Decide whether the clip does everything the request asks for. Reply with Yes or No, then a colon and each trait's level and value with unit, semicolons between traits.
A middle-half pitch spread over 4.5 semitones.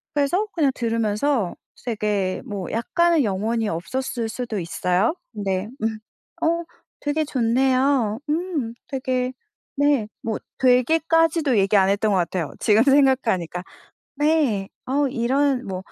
Yes: wide, 5.5 semitones